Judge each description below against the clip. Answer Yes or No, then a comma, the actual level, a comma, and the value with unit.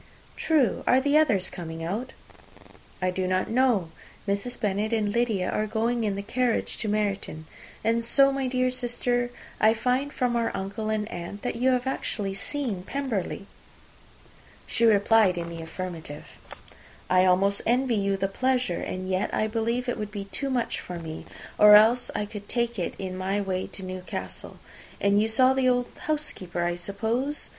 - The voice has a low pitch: No, high, 215 Hz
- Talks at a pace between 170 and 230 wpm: Yes, average, 175 wpm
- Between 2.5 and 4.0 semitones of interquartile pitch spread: No, average, 4.4 semitones